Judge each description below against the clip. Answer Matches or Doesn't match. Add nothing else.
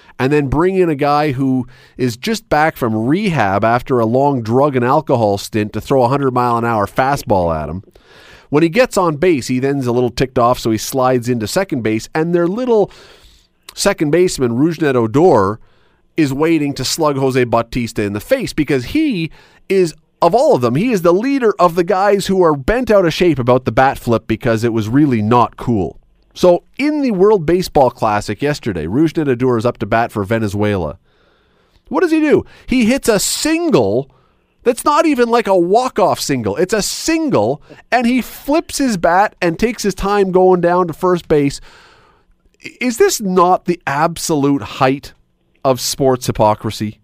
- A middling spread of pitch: Doesn't match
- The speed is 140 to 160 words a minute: Doesn't match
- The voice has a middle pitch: Matches